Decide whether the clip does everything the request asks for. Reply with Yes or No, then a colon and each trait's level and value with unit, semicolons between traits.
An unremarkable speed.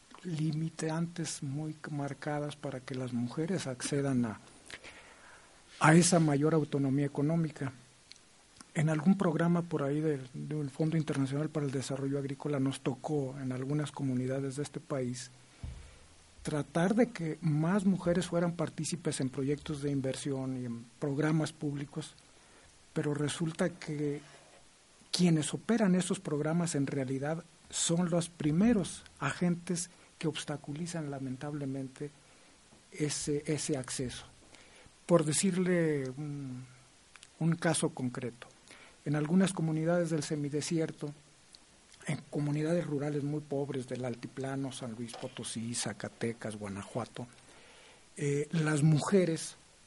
No: slow, 115 wpm